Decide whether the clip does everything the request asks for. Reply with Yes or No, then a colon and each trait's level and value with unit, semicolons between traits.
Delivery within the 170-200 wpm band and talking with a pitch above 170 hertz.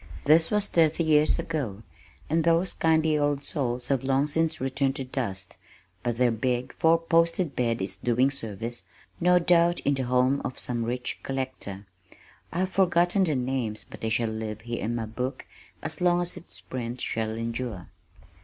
No: average, 175 wpm; low, 135 Hz